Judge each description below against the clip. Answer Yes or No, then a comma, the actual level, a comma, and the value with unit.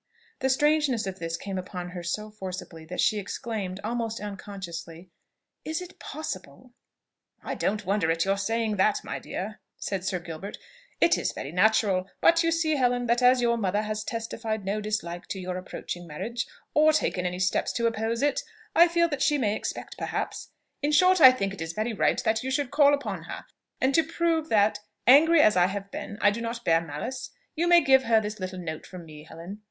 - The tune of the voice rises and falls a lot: Yes, wide, 5.9 semitones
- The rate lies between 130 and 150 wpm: No, fast, 205 wpm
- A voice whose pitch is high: Yes, high, 215 Hz